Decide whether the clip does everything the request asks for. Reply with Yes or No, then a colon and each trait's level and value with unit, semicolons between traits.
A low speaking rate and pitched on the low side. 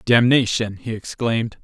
Yes: slow, 110 wpm; low, 115 Hz